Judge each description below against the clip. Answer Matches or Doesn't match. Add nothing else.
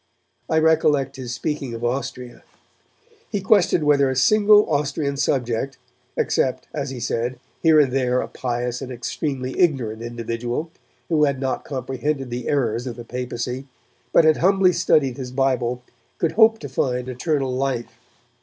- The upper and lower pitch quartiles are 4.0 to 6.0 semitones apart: Doesn't match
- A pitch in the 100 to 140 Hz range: Matches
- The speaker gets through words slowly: Doesn't match